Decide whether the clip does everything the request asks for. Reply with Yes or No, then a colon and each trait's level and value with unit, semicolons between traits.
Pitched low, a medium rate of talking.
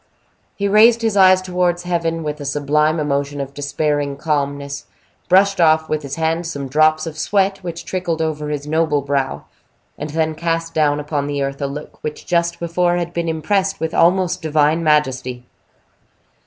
No: medium, 155 Hz; average, 170 wpm